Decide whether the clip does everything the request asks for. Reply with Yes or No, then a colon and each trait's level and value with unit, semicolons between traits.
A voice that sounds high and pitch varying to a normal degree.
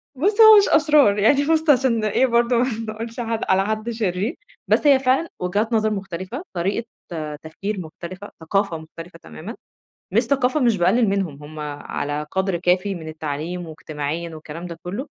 No: high, 200 Hz; wide, 6.0 semitones